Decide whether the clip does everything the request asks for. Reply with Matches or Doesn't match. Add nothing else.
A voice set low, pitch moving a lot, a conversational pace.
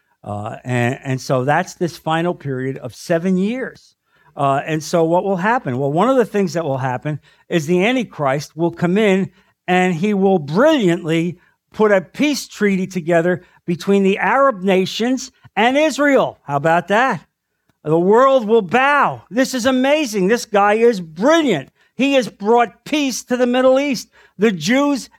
Doesn't match